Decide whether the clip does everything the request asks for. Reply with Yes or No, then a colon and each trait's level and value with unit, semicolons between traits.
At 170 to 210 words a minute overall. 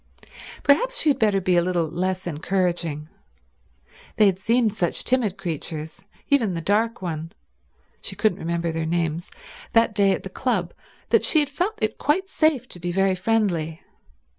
No: average, 160 wpm